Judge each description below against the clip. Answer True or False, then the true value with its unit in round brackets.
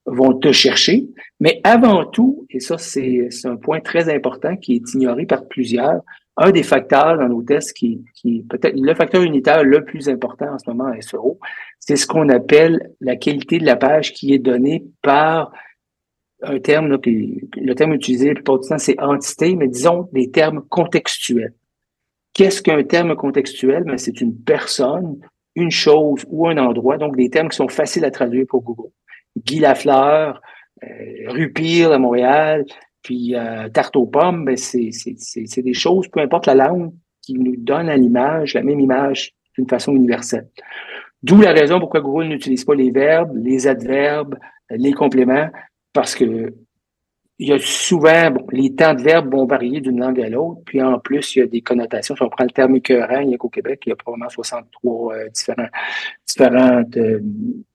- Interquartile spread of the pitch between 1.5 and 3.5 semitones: False (4.2 semitones)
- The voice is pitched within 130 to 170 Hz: True (140 Hz)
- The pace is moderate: True (190 wpm)